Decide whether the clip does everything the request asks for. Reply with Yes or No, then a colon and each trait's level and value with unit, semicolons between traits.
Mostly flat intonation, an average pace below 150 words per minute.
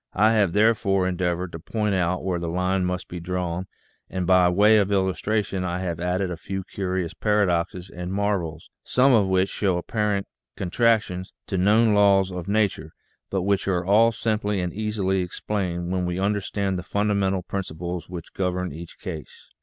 No: narrow, 2.3 semitones; average, 170 wpm